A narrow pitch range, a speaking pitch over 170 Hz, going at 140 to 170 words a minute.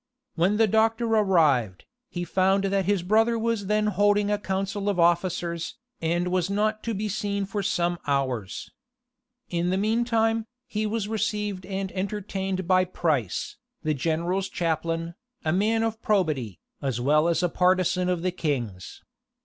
No: average, 3.7 semitones; high, 190 Hz; average, 155 wpm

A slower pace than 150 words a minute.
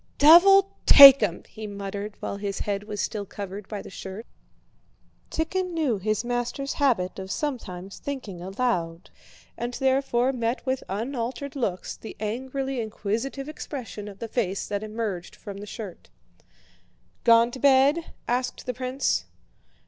Yes: average, 140 wpm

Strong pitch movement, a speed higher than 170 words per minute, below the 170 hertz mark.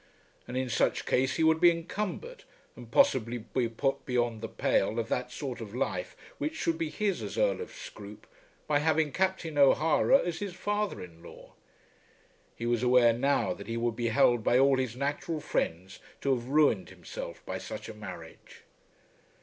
Yes: wide, 7.2 semitones; average, 180 wpm; medium, 140 Hz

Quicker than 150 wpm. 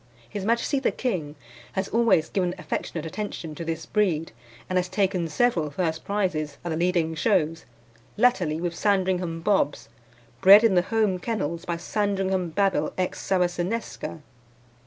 No: average, 145 wpm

